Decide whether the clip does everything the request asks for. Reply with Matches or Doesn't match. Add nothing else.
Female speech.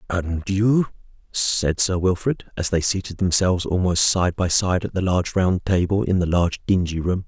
Doesn't match